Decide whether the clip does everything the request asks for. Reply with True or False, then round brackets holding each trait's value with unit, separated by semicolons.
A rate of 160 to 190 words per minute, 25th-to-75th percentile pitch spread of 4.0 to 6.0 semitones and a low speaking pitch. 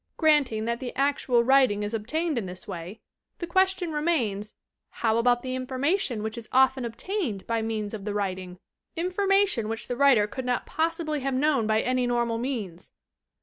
False (175 wpm; 5.3 semitones; 245 Hz)